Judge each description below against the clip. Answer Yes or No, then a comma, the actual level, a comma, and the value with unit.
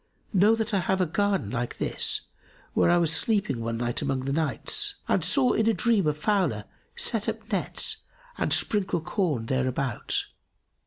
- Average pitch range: No, wide, 7.5 semitones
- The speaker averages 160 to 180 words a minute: Yes, average, 170 wpm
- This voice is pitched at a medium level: Yes, medium, 175 Hz